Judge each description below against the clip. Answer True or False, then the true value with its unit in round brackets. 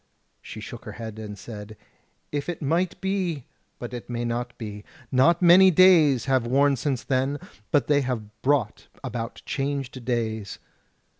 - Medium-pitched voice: False (130 Hz)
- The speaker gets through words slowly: False (155 wpm)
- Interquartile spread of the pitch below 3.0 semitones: False (4.0 semitones)